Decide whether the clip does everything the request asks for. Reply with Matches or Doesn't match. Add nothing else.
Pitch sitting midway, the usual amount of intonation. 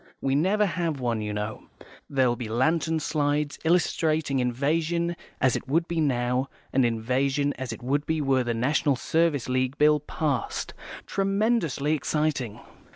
Matches